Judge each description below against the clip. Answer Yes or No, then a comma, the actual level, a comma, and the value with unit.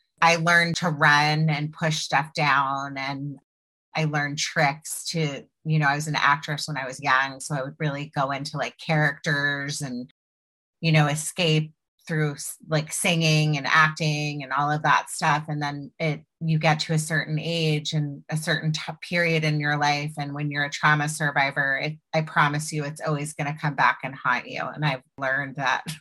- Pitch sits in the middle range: Yes, medium, 150 Hz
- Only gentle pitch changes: Yes, narrow, 1.7 semitones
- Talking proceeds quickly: No, average, 195 wpm